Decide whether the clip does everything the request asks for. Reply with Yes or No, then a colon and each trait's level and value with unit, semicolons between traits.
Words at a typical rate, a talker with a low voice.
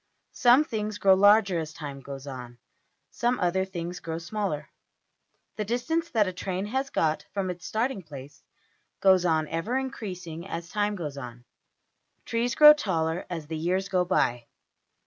No: average, 160 wpm; medium, 180 Hz